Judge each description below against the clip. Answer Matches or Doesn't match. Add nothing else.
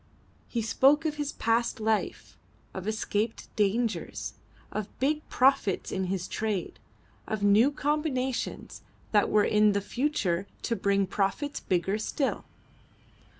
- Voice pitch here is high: Matches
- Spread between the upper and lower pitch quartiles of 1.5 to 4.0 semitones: Doesn't match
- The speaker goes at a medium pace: Doesn't match